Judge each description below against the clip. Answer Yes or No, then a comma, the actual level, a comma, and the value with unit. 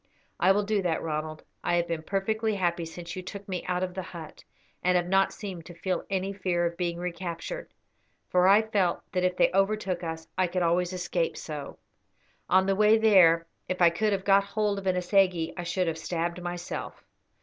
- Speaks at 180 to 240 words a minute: Yes, fast, 205 wpm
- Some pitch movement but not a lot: No, narrow, 2.3 semitones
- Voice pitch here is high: No, medium, 180 Hz